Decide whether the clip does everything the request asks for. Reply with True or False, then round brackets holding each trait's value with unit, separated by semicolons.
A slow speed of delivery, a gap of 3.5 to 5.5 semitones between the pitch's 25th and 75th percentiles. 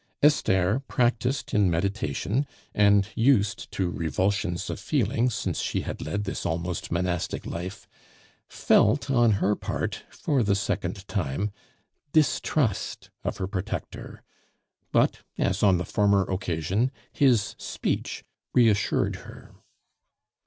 True (115 wpm; 4.4 semitones)